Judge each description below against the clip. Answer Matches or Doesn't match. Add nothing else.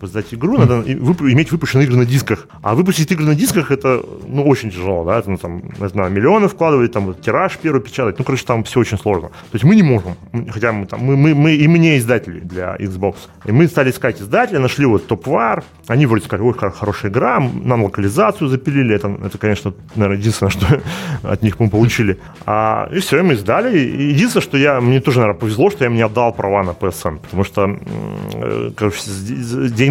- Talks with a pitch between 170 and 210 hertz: Doesn't match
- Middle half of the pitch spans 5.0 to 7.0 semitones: Matches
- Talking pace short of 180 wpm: Doesn't match